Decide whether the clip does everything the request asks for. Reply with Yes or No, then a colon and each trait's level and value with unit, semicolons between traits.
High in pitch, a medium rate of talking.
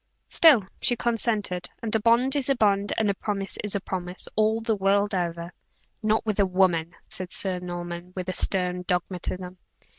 Yes: high, 195 Hz; average, 170 wpm